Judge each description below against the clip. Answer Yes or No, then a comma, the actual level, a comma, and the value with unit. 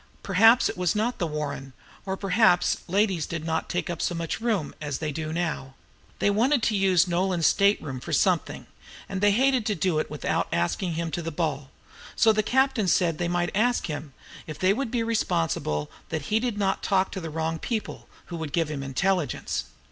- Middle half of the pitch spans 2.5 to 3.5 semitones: No, average, 4.6 semitones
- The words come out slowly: No, fast, 205 wpm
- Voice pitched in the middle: Yes, medium, 175 Hz